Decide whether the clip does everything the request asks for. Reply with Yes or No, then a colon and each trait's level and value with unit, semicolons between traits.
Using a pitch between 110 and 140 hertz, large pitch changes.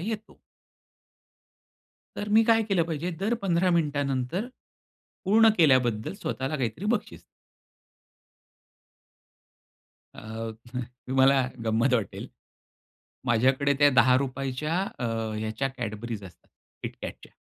Yes: low, 135 Hz; wide, 6.5 semitones